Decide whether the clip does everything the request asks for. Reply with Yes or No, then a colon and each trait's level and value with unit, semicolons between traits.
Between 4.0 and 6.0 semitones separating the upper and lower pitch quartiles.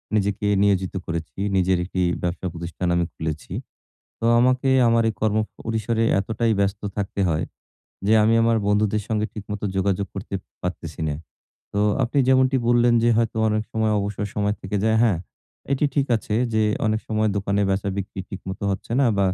No: average, 2.7 semitones